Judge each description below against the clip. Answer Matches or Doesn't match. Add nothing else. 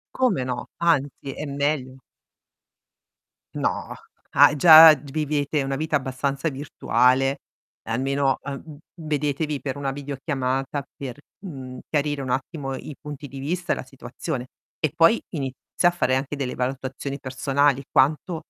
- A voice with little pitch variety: Matches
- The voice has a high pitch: Doesn't match